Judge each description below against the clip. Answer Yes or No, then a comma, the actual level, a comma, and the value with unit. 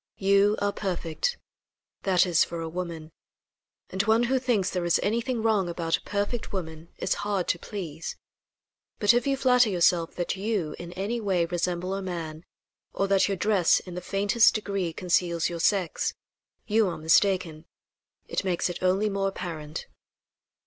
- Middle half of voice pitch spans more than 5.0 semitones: No, average, 3.2 semitones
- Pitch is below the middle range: No, high, 190 Hz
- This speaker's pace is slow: No, average, 165 wpm